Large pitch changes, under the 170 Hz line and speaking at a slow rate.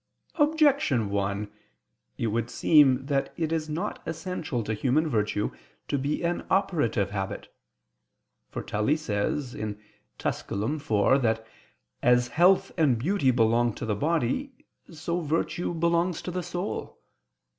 Yes: wide, 7.1 semitones; medium, 140 Hz; slow, 130 wpm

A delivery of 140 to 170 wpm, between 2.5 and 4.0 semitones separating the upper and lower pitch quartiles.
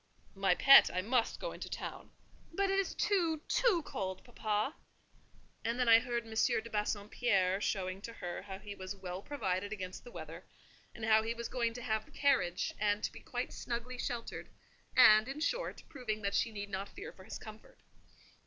No: average, 190 wpm; average, 3.7 semitones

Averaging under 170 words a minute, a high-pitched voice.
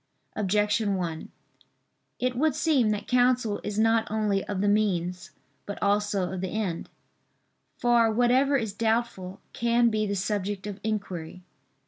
Yes: average, 140 wpm; high, 210 Hz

